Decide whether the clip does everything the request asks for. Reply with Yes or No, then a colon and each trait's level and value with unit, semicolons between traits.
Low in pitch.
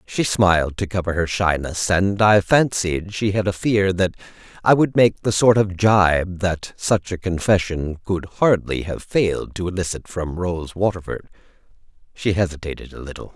Yes: very low, 95 Hz